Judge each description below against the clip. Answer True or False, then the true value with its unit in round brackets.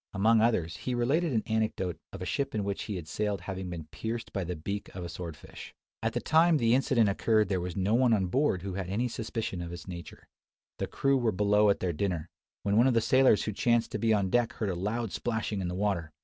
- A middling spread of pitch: True (4.2 semitones)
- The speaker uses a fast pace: True (250 wpm)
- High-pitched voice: False (105 Hz)